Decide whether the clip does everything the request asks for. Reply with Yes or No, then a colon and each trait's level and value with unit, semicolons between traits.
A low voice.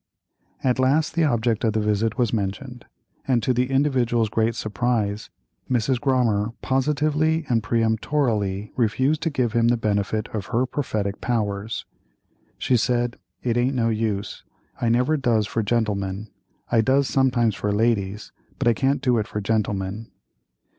Yes: low, 115 Hz